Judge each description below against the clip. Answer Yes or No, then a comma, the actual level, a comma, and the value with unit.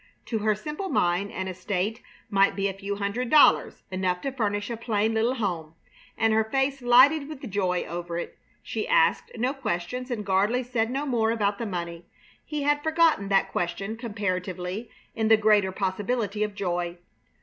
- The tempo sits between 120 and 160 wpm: No, average, 175 wpm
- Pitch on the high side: Yes, high, 210 Hz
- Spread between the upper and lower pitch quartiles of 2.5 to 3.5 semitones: No, average, 4.6 semitones